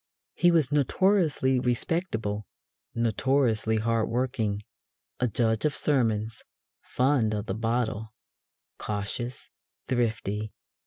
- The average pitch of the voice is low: Yes, low, 115 Hz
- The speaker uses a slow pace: Yes, slow, 95 wpm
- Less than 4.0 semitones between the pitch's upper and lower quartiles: Yes, average, 3.4 semitones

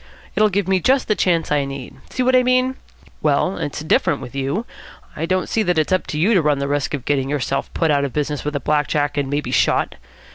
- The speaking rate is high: Yes, fast, 250 wpm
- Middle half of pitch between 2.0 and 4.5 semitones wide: No, average, 5.0 semitones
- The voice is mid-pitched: Yes, medium, 150 Hz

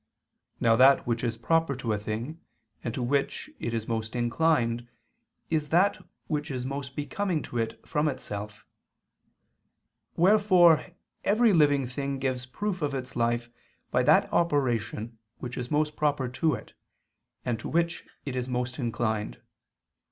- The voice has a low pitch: Yes, low, 130 Hz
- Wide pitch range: No, average, 4.4 semitones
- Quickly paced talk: No, average, 150 wpm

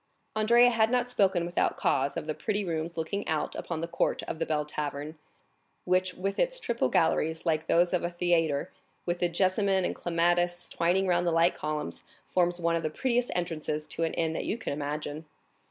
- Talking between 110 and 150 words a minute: No, average, 200 wpm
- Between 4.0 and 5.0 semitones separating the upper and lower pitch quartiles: No, average, 2.9 semitones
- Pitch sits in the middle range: Yes, medium, 175 Hz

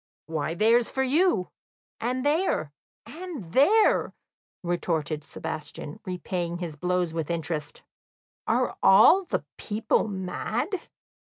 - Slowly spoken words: Yes, slow, 105 wpm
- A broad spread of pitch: Yes, wide, 8.0 semitones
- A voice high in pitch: No, medium, 180 Hz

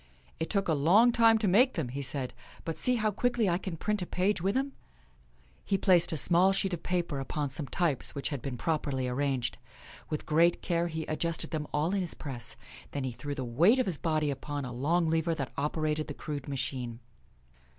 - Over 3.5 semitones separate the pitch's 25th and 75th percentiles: Yes, average, 4.7 semitones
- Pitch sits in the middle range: Yes, medium, 160 Hz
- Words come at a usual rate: No, fast, 215 wpm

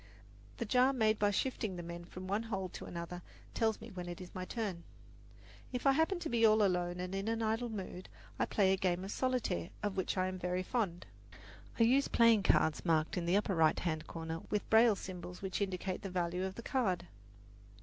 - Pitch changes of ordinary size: Yes, average, 4.0 semitones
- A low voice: No, high, 190 Hz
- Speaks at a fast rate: Yes, fast, 215 wpm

